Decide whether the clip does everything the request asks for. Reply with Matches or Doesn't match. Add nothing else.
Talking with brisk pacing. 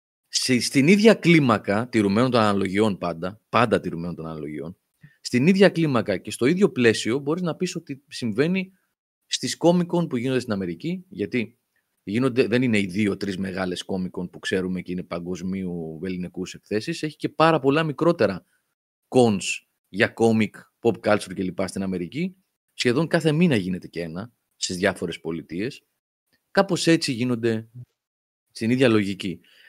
Doesn't match